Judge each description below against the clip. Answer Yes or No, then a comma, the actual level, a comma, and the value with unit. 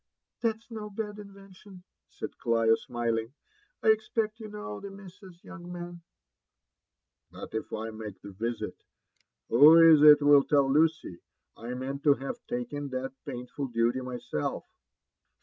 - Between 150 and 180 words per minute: No, average, 140 wpm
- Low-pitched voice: No, medium, 145 Hz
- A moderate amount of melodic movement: No, wide, 8.4 semitones